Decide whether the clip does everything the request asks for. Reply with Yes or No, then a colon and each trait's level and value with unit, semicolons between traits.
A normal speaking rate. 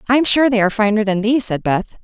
No: fast, 265 wpm